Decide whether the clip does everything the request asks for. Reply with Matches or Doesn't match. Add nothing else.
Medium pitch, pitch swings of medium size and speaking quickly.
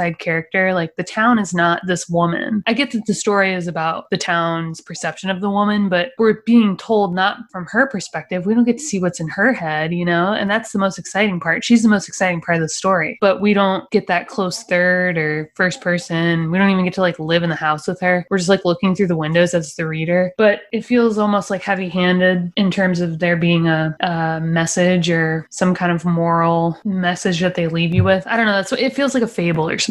Matches